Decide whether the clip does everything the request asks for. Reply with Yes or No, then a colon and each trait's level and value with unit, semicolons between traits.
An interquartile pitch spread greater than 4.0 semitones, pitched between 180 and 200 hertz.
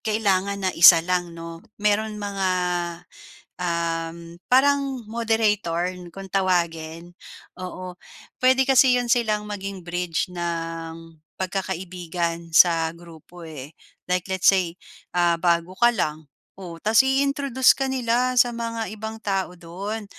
Yes: average, 4.7 semitones; medium, 185 Hz